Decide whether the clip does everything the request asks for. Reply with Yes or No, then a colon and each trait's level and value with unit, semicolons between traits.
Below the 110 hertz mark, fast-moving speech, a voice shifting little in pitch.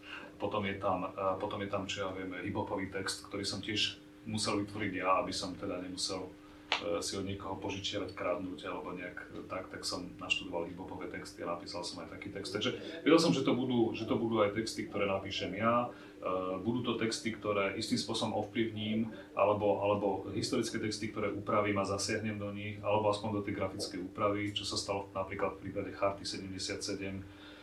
Yes: low, 100 Hz; fast, 180 wpm; narrow, 1.4 semitones